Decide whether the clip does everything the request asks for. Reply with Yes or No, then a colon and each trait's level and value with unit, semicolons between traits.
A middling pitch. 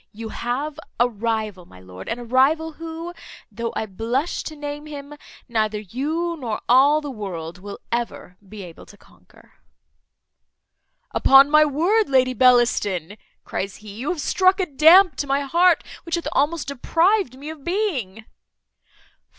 No: very high, 265 Hz